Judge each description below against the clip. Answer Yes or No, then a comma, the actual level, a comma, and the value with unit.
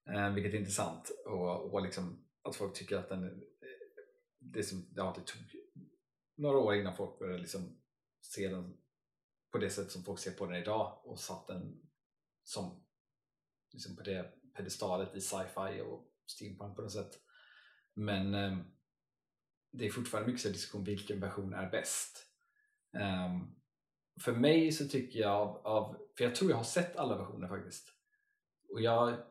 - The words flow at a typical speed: Yes, average, 160 wpm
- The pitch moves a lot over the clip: Yes, wide, 7.0 semitones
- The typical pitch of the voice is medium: No, low, 105 Hz